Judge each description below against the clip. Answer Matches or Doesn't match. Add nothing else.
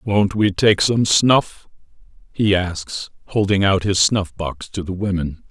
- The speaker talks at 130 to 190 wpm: Matches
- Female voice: Doesn't match